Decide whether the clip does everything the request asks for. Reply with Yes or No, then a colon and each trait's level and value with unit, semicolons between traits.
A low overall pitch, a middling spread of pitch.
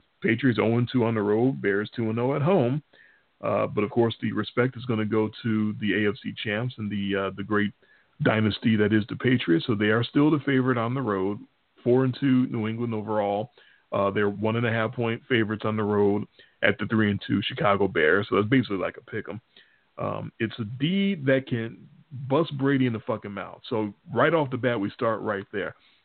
Yes: low, 115 Hz; average, 3.5 semitones